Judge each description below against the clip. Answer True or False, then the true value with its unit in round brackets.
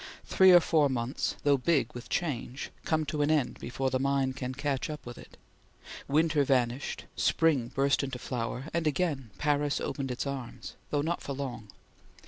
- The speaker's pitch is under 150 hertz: True (140 Hz)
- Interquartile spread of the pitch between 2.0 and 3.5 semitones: True (2.8 semitones)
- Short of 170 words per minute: False (175 wpm)